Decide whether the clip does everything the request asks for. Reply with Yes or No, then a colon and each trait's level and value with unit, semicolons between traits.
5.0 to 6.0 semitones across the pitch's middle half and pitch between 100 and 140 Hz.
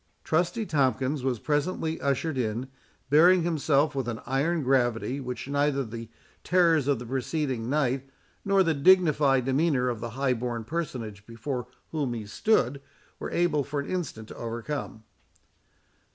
No: average, 4.3 semitones; low, 135 Hz